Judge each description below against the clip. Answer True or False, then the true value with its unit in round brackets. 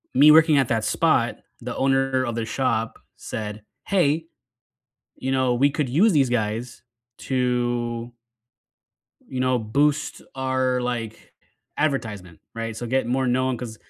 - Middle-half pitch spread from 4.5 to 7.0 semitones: False (2.5 semitones)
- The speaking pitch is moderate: False (125 Hz)